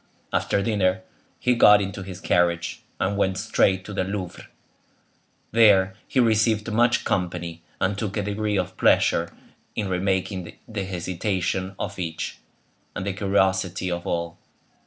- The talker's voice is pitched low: Yes, very low, 95 Hz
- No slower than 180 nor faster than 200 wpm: No, average, 140 wpm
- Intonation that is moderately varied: No, narrow, 2.2 semitones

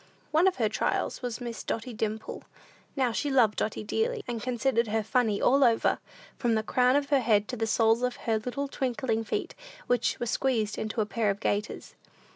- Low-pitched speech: No, high, 235 Hz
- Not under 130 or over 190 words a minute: No, average, 200 wpm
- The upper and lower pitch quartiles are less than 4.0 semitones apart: Yes, average, 2.8 semitones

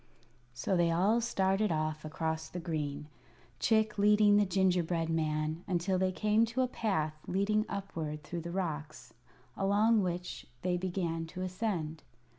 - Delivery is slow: No, average, 145 wpm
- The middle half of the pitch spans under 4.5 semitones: Yes, average, 4.0 semitones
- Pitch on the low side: No, medium, 180 Hz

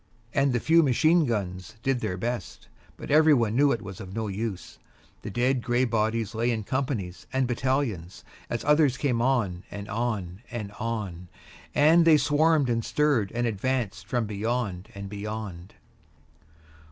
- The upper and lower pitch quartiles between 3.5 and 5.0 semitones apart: Yes, average, 4.6 semitones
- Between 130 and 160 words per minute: Yes, average, 155 wpm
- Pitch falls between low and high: No, low, 115 Hz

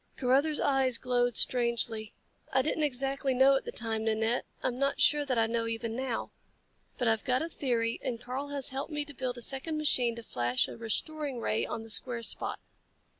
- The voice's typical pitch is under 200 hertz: No, very high, 250 Hz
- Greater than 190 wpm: Yes, average, 200 wpm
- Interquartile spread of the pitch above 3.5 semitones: No, average, 3.1 semitones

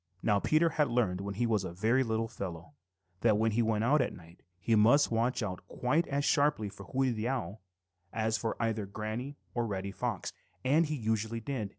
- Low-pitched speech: Yes, low, 115 Hz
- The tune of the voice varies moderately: Yes, average, 3.5 semitones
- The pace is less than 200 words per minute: No, fast, 205 wpm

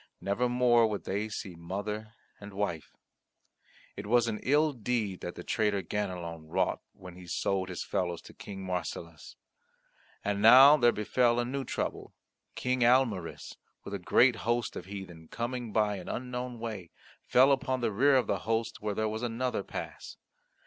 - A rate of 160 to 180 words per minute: Yes, average, 170 wpm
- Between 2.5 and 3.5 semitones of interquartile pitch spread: No, average, 4.2 semitones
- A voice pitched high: No, low, 110 Hz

